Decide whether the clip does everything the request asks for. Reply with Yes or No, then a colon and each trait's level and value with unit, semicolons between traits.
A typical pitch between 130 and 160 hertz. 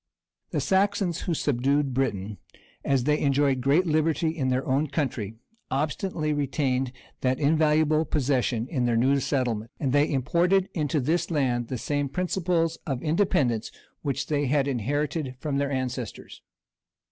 Yes: medium, 140 Hz